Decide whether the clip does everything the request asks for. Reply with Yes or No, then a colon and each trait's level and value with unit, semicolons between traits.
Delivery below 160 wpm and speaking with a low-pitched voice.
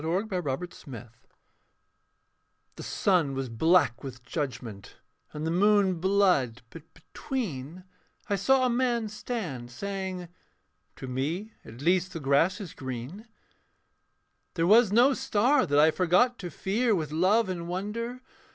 No: slow, 135 wpm; medium, 180 Hz